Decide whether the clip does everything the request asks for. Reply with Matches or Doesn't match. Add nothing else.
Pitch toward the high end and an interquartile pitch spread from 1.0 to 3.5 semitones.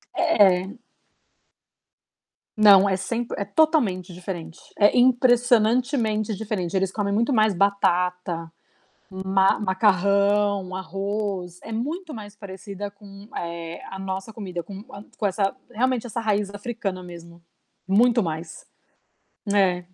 Matches